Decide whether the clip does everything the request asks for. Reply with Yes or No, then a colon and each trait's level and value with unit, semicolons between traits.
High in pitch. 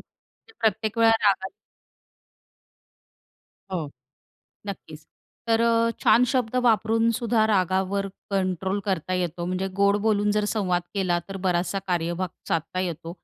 Yes: high, 195 Hz